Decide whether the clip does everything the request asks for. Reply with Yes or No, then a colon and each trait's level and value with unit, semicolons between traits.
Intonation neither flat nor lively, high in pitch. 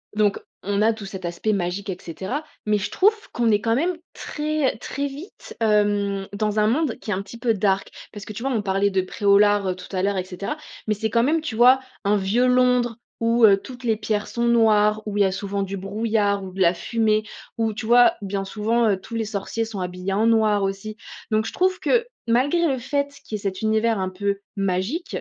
Yes: average, 3.0 semitones; high, 215 Hz